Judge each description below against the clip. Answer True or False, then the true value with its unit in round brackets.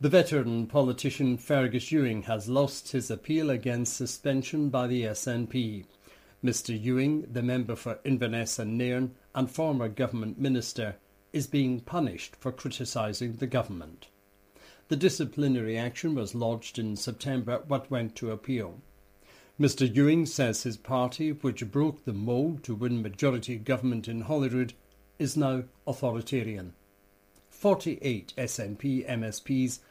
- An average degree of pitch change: True (3.5 semitones)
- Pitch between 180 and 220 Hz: False (125 Hz)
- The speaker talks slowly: True (130 wpm)